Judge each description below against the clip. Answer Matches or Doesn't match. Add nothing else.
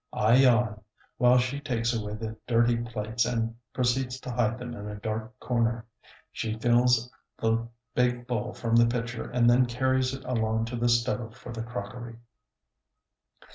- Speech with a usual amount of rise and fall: Doesn't match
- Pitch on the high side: Doesn't match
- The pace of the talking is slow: Doesn't match